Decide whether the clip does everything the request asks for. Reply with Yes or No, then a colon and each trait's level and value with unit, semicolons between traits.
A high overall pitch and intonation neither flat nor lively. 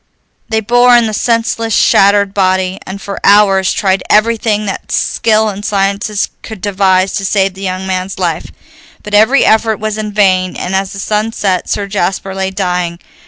No: high, 200 Hz; narrow, 2.1 semitones